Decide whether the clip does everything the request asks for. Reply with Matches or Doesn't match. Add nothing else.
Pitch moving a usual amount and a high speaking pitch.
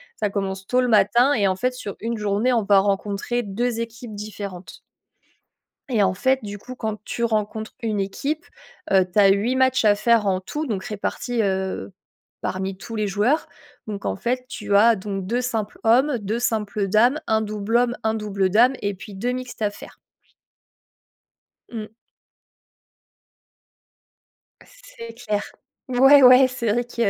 Matches